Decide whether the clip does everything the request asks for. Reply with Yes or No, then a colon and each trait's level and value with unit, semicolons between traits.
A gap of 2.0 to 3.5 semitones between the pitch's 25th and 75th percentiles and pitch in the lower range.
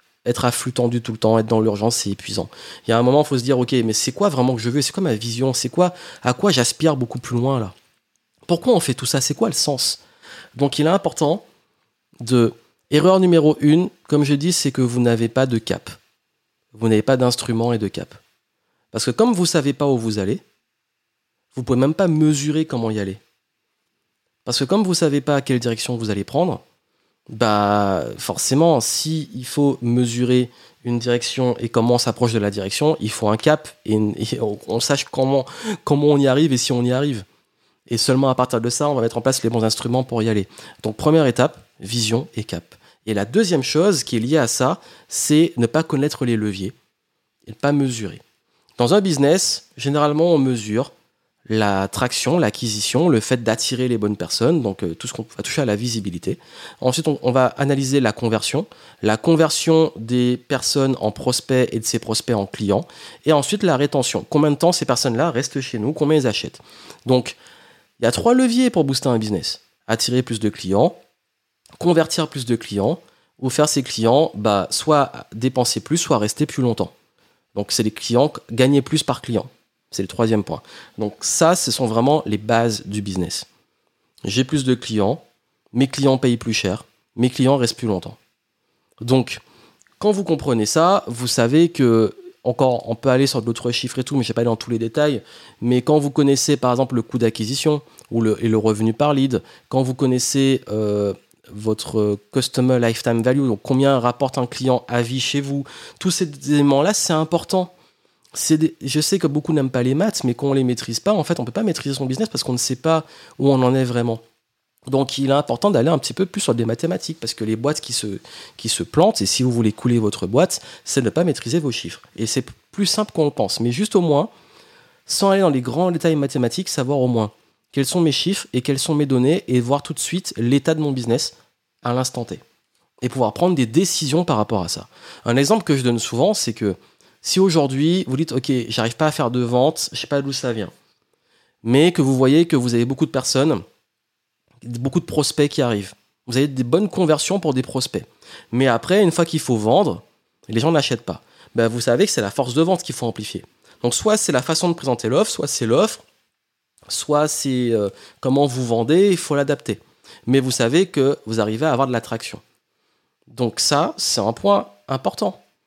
No: average, 4.6 semitones; low, 130 Hz